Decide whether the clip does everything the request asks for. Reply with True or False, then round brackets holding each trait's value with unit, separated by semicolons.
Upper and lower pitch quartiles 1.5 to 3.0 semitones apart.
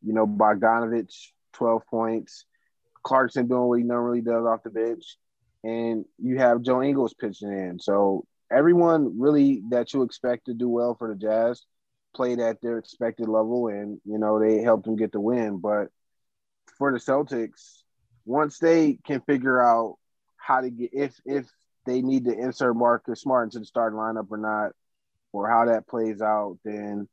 True (2.5 semitones)